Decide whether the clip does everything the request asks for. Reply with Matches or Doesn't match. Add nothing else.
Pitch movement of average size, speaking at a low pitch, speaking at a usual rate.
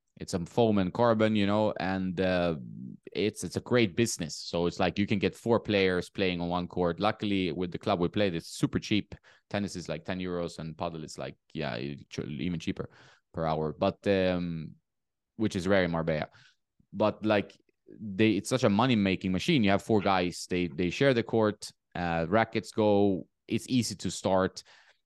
Matches